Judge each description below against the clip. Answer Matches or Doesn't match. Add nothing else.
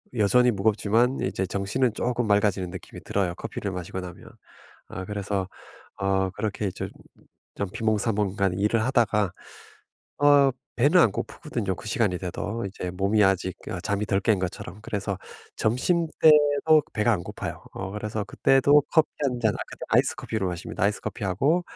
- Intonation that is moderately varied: Matches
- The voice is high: Doesn't match